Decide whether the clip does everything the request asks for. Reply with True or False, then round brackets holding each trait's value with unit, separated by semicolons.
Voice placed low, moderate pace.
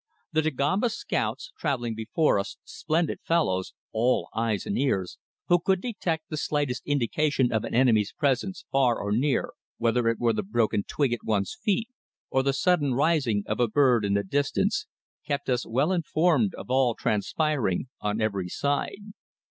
True (130 Hz; 165 wpm)